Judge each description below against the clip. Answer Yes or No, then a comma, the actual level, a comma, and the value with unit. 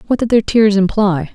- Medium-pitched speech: No, high, 205 Hz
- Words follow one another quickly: Yes, fast, 225 wpm